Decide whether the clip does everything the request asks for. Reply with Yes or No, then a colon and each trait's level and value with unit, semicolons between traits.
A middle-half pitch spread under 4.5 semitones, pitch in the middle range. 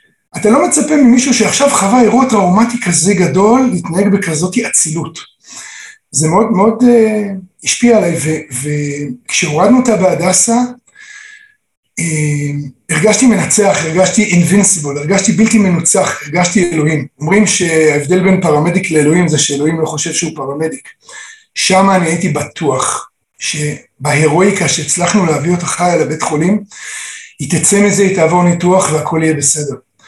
No: wide, 5.6 semitones; medium, 180 Hz